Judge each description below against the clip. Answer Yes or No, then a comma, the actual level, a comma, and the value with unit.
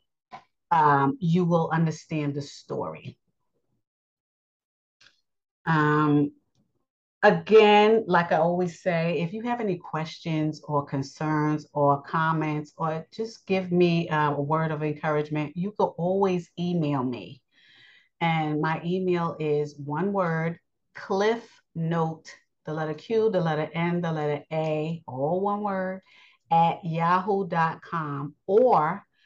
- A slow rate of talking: Yes, slow, 115 wpm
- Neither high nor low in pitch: Yes, medium, 165 Hz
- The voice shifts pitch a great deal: No, average, 3.0 semitones